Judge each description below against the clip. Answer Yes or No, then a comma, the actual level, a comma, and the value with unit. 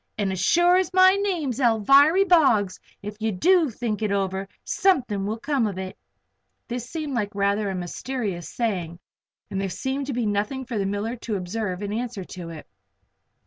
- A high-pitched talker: Yes, high, 220 Hz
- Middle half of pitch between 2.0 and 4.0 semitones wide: No, wide, 5.6 semitones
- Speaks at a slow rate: No, average, 185 wpm